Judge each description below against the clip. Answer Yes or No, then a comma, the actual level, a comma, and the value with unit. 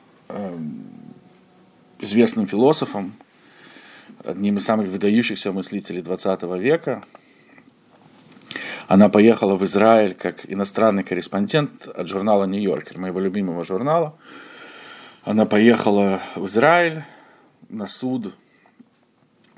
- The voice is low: Yes, low, 105 Hz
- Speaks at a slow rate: Yes, slow, 85 wpm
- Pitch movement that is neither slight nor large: Yes, average, 4.9 semitones